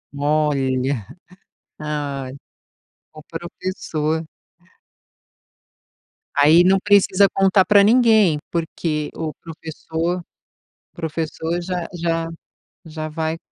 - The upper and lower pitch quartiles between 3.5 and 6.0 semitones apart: No, average, 2.8 semitones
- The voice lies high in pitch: No, medium, 165 Hz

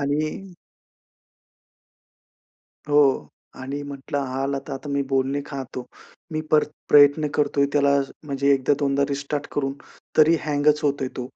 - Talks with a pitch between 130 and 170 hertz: Yes, medium, 140 Hz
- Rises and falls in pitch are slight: Yes, narrow, 1.2 semitones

